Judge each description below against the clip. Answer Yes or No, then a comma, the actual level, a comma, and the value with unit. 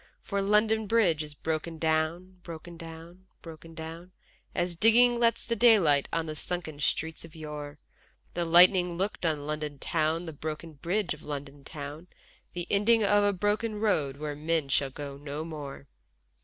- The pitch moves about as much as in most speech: Yes, average, 3.7 semitones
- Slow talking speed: No, average, 165 wpm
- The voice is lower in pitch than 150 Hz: No, medium, 165 Hz